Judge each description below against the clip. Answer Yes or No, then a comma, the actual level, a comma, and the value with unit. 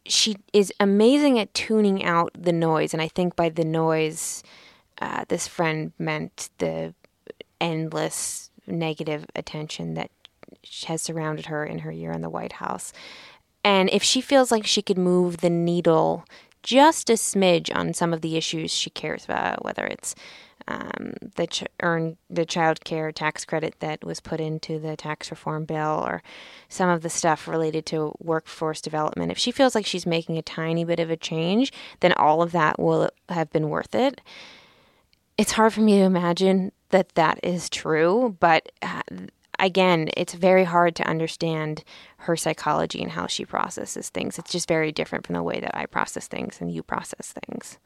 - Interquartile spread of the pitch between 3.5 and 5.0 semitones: No, average, 3.1 semitones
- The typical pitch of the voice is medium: Yes, medium, 165 Hz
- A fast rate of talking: No, average, 180 wpm